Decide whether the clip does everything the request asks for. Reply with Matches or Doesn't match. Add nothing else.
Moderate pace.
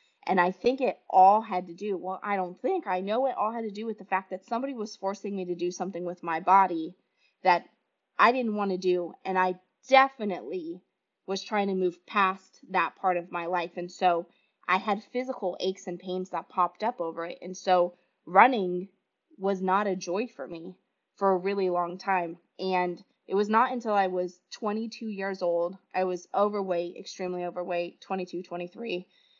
Matches